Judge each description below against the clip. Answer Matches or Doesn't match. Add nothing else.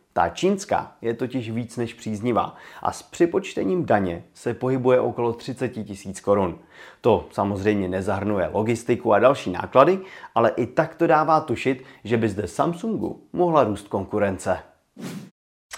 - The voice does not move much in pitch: Doesn't match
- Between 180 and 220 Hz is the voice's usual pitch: Doesn't match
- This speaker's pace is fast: Doesn't match